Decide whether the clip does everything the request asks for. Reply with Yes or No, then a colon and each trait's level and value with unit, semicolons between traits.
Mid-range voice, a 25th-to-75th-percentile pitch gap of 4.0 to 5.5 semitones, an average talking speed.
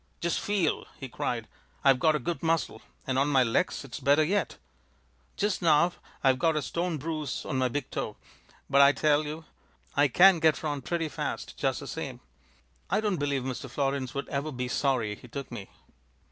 No: medium, 145 Hz; average, 3.6 semitones; average, 190 wpm